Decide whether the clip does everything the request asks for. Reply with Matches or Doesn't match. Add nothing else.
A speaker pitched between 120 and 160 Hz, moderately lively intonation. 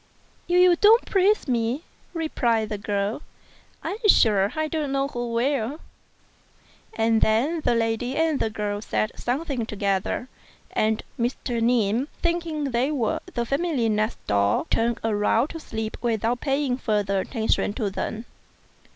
Doesn't match